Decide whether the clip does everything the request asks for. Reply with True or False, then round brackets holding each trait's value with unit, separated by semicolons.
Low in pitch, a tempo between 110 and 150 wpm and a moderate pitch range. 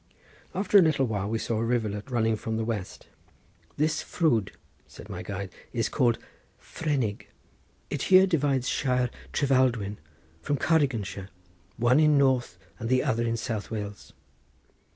True (120 Hz; 145 wpm; 4.2 semitones)